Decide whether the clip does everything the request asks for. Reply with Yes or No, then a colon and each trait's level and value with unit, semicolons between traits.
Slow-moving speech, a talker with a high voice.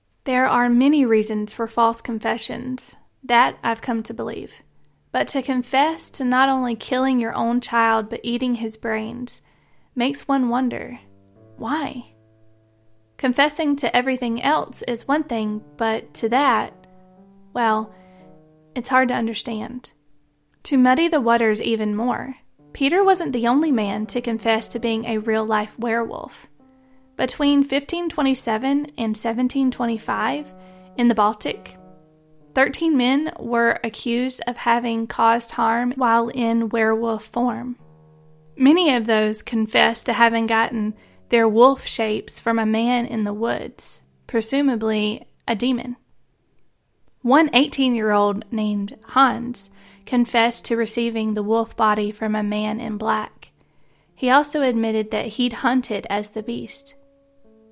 Yes: slow, 130 wpm; high, 235 Hz